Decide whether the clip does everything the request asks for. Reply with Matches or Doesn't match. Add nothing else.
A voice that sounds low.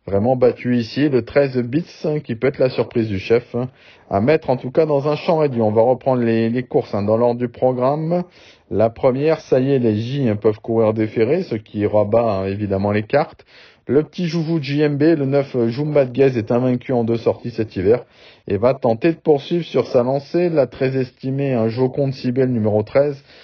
Matches